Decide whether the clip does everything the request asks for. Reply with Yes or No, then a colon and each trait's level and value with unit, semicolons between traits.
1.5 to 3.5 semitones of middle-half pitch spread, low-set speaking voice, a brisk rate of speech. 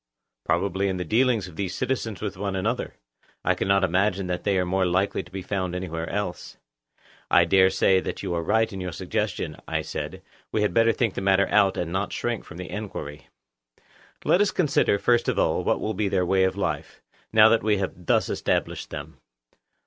Yes: narrow, 2.6 semitones; very low, 95 Hz; fast, 210 wpm